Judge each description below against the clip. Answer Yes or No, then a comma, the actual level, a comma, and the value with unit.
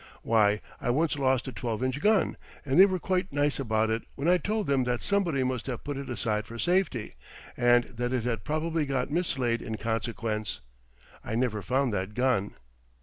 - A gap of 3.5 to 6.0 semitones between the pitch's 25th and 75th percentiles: Yes, average, 4.4 semitones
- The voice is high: No, low, 125 Hz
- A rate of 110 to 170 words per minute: No, average, 195 wpm